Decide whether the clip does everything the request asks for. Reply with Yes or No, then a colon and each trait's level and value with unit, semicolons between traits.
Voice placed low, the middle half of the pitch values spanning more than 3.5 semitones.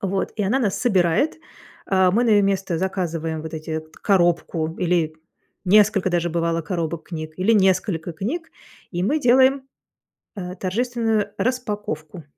No: medium, 185 Hz; average, 4.2 semitones